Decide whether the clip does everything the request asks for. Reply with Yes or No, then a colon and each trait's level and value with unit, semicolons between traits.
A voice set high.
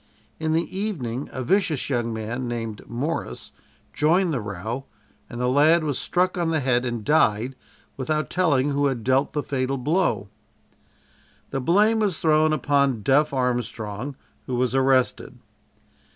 No: low, 135 Hz